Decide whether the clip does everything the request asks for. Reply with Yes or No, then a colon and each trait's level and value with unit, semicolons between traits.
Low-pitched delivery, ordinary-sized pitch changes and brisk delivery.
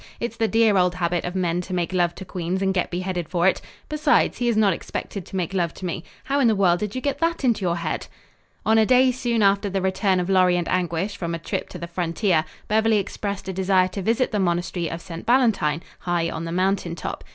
No: medium, 185 Hz; average, 3.6 semitones; fast, 245 wpm